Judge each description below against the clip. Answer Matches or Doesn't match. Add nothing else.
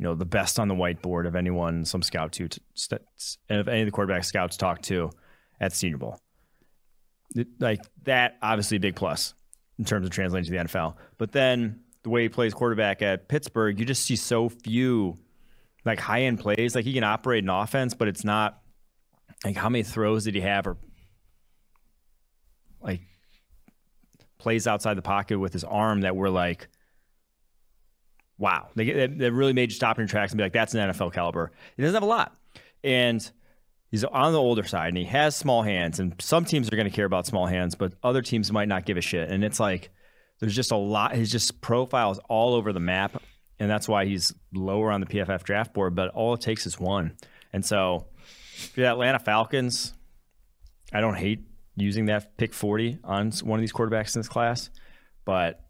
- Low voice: Matches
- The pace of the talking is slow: Doesn't match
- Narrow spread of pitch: Doesn't match